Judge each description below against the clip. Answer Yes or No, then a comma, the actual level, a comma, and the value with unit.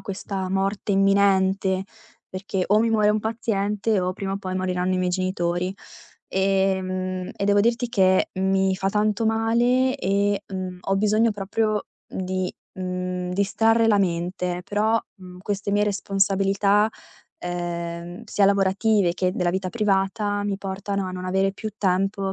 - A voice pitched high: Yes, high, 195 Hz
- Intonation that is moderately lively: No, narrow, 1.9 semitones